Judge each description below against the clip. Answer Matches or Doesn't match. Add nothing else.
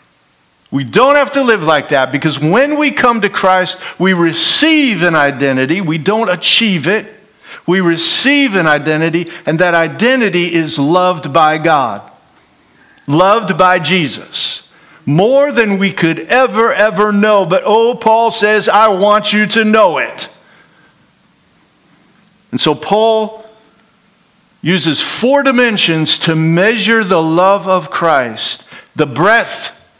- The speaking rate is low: Matches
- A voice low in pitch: Doesn't match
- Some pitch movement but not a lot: Matches